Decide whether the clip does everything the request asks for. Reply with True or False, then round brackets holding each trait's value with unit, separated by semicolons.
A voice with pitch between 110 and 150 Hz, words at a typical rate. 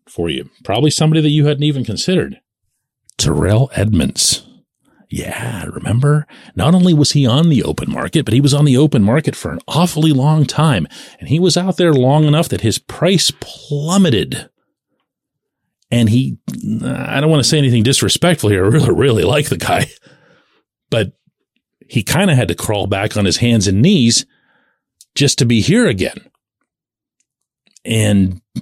True (140 Hz; 165 wpm)